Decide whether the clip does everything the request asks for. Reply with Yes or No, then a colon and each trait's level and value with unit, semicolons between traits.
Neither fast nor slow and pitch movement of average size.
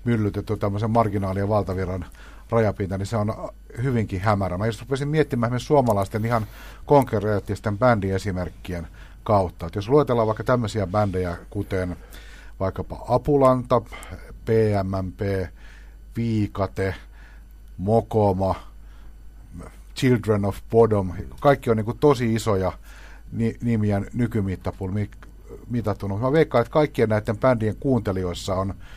Yes: average, 105 wpm; average, 3.4 semitones